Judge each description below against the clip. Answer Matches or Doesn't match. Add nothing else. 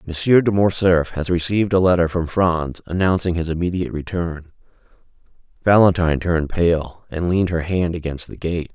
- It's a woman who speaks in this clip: Doesn't match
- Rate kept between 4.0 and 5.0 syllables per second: Doesn't match